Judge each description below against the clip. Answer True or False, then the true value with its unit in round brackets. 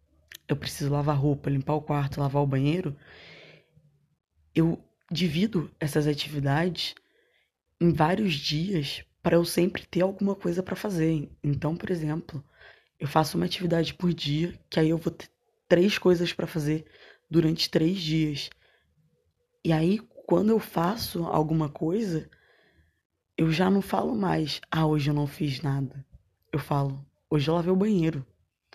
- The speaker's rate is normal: True (150 wpm)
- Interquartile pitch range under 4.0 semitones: True (3.4 semitones)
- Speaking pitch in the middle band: True (160 Hz)